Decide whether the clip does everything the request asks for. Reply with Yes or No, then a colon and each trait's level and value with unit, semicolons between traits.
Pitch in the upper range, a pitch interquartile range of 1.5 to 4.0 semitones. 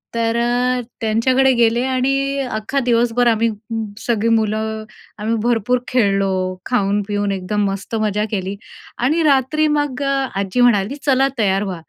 Yes: high, 230 Hz; average, 3.7 semitones